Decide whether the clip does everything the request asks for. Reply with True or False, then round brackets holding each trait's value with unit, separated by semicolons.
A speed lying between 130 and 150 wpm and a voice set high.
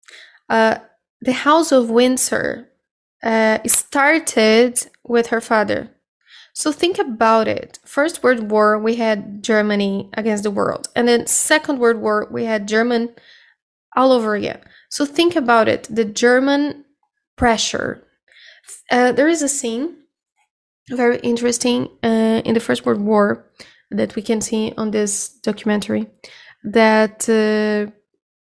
True (135 wpm; 230 Hz)